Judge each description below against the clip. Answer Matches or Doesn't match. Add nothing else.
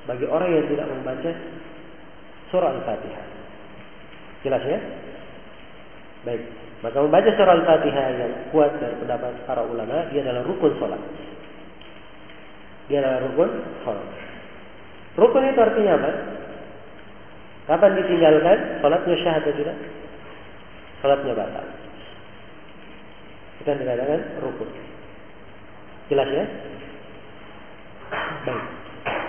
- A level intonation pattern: Doesn't match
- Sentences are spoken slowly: Doesn't match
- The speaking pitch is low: Doesn't match